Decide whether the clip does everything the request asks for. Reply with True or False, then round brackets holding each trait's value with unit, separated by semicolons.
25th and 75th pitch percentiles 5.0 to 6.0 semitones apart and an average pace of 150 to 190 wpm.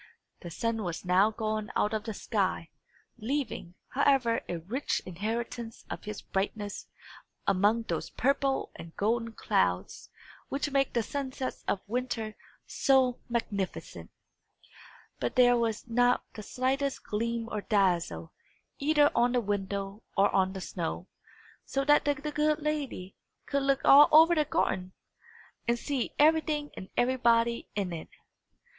False (5.3 semitones; 140 wpm)